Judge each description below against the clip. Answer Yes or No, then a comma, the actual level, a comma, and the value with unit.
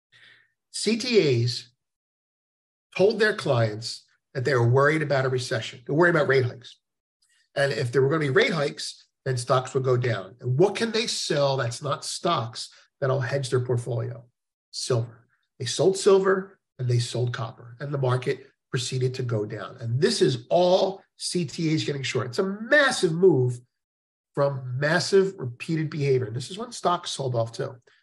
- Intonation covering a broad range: Yes, wide, 5.9 semitones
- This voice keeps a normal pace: Yes, average, 170 wpm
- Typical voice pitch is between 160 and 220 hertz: No, low, 135 Hz